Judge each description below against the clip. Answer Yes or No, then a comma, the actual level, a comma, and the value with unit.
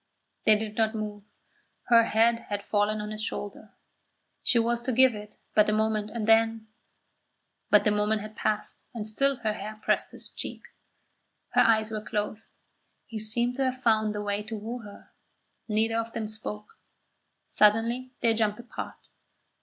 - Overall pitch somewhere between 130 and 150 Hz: No, high, 220 Hz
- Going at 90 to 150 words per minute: No, average, 170 wpm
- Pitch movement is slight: Yes, narrow, 1.4 semitones